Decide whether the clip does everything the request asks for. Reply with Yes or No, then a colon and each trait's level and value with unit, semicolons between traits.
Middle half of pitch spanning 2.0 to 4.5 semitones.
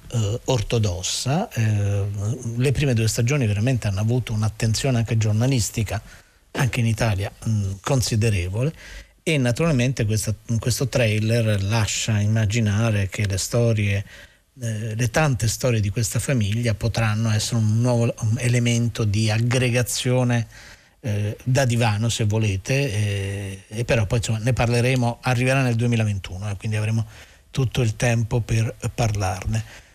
Yes: narrow, 2.4 semitones